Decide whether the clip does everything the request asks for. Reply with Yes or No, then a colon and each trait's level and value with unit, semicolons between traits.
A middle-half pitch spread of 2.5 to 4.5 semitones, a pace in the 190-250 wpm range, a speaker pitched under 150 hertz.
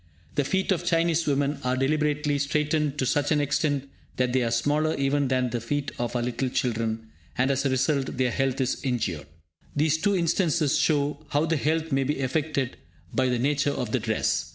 Yes: average, 2.9 semitones; average, 200 wpm; medium, 140 Hz